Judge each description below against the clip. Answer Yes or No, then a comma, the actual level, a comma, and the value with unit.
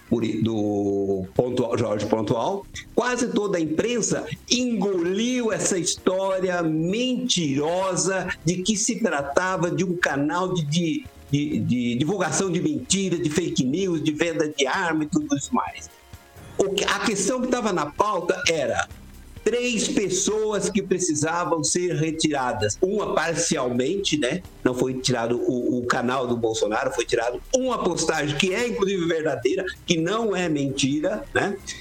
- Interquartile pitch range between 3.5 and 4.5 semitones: No, wide, 5.4 semitones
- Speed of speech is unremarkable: Yes, average, 140 wpm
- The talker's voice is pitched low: No, medium, 175 Hz